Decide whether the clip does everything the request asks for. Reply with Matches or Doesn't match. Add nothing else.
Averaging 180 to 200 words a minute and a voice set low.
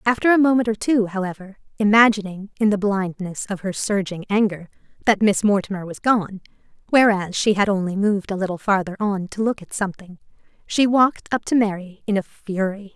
Doesn't match